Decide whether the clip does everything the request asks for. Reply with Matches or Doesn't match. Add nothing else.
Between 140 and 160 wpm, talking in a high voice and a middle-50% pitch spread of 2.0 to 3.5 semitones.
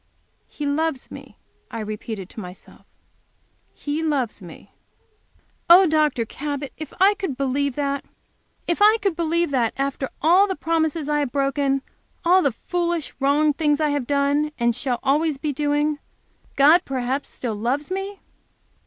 Matches